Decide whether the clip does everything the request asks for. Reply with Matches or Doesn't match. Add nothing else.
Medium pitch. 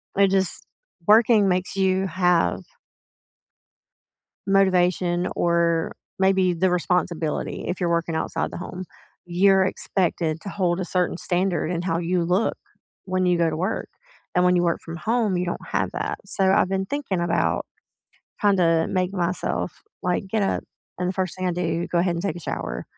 Matches